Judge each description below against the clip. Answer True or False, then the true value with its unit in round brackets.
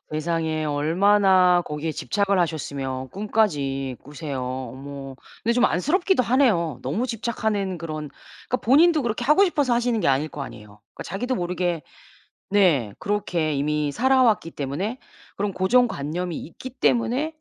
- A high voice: False (180 Hz)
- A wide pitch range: True (7.8 semitones)